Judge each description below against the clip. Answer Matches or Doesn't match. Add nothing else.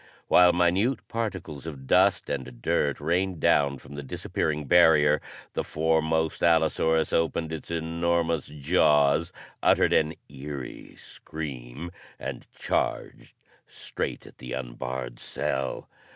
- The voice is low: Matches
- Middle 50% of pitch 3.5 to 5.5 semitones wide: Doesn't match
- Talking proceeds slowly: Matches